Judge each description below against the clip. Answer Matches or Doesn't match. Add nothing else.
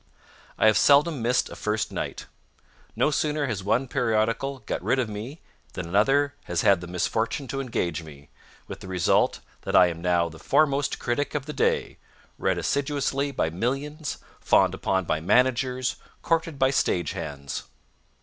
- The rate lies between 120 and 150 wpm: Doesn't match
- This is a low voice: Matches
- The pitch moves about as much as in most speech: Doesn't match